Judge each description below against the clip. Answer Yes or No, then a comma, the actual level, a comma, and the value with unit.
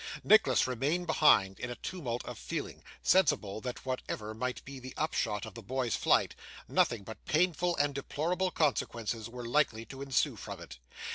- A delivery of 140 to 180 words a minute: Yes, average, 165 wpm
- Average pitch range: Yes, average, 4.8 semitones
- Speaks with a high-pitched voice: No, low, 130 Hz